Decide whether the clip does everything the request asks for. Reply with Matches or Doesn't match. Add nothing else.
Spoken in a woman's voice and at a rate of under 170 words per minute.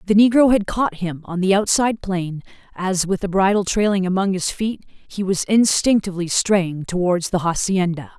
Doesn't match